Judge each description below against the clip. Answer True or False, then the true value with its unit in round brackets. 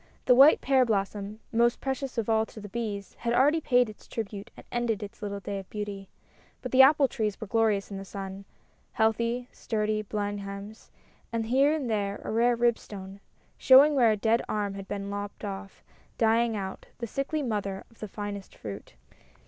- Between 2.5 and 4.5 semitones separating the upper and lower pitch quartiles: True (3.0 semitones)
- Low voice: False (215 Hz)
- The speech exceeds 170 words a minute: True (190 wpm)